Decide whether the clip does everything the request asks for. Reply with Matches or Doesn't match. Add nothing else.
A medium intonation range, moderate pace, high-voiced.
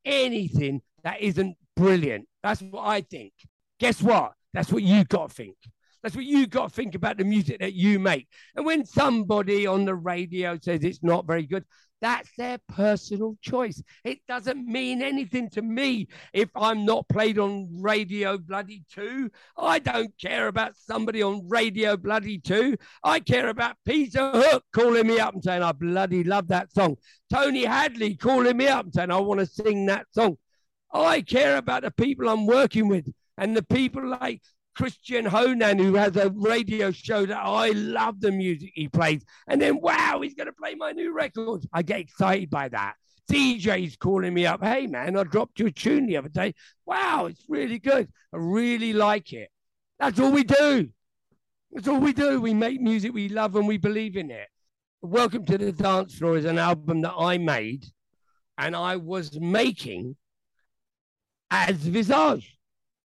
Matches